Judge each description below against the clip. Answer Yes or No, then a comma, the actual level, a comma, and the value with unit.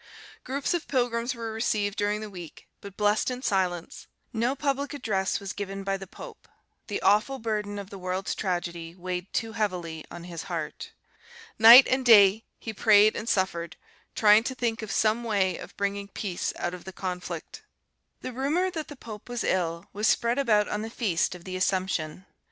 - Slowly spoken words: No, average, 185 wpm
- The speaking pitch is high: Yes, high, 205 Hz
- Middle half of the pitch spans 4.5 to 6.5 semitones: No, average, 3.8 semitones